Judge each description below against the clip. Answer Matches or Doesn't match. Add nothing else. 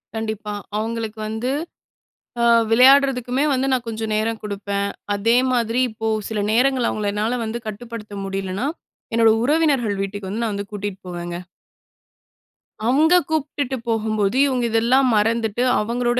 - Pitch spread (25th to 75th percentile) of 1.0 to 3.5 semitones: Matches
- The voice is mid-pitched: Doesn't match